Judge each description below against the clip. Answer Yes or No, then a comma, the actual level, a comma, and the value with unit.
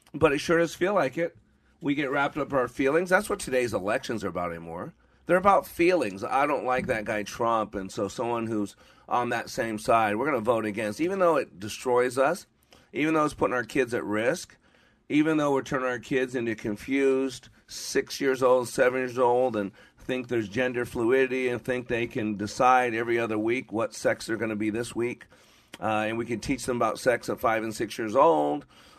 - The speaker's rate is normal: No, fast, 215 wpm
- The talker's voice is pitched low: Yes, low, 125 Hz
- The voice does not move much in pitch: No, average, 3.3 semitones